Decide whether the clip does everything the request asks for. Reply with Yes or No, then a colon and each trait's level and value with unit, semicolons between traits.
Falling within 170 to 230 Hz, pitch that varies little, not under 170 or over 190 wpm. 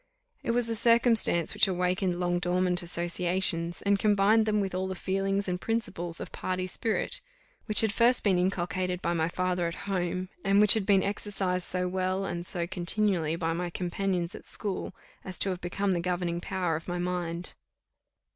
Yes: medium, 185 Hz; narrow, 2.1 semitones; average, 185 wpm